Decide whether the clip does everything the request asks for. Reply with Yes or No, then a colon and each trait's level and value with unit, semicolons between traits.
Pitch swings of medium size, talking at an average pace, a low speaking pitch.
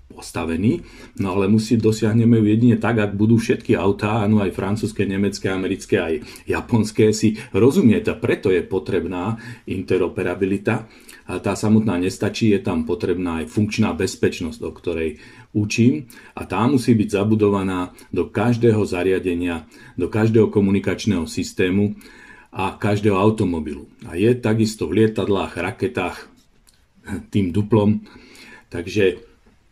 No: narrow, 2.1 semitones; average, 125 wpm; low, 105 Hz